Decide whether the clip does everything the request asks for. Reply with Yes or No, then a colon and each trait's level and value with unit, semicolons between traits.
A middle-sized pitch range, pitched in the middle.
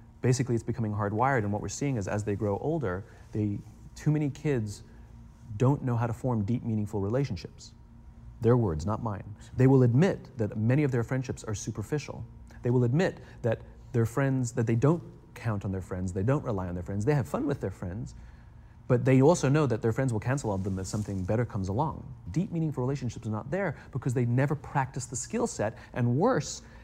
No: average, 3.9 semitones; low, 120 Hz